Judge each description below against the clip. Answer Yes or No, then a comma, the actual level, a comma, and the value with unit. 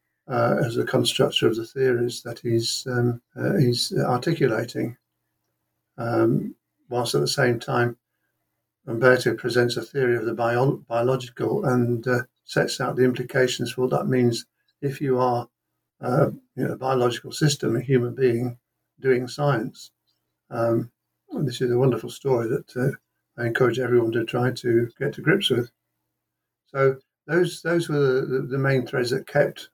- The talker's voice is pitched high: No, low, 125 Hz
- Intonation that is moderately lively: No, narrow, 1.9 semitones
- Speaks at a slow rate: No, average, 160 wpm